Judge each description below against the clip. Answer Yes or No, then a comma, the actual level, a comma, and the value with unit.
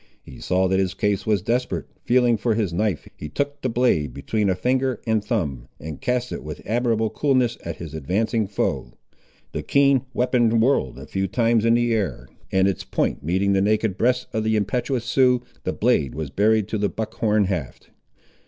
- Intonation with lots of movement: No, average, 4.3 semitones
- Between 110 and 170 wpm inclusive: No, average, 195 wpm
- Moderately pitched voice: No, low, 110 Hz